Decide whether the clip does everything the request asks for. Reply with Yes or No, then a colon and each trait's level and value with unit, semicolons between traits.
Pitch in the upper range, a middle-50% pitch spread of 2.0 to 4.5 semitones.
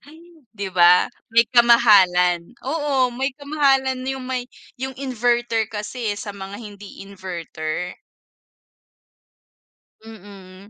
No: high, 225 Hz; average, 5.1 semitones